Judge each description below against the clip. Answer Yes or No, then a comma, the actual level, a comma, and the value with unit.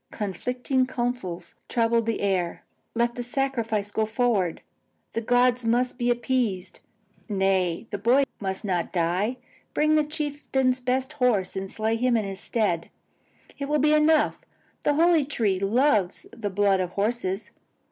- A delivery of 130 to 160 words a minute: Yes, average, 145 wpm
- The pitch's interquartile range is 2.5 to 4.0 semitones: No, average, 4.6 semitones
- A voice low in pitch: No, high, 230 Hz